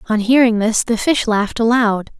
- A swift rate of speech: No, average, 190 wpm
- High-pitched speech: Yes, high, 230 Hz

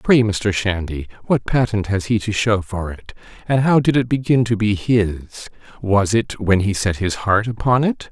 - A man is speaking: Yes, male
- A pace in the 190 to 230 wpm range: Yes, fast, 205 wpm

